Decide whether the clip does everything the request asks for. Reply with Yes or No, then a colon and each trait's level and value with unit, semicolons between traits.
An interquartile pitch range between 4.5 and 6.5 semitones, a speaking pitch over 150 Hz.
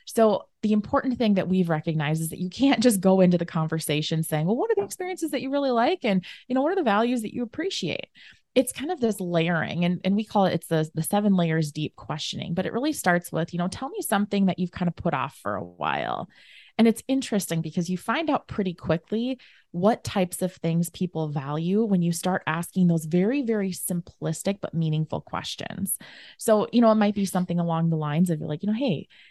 Yes: average, 5.1 semitones; medium, 185 Hz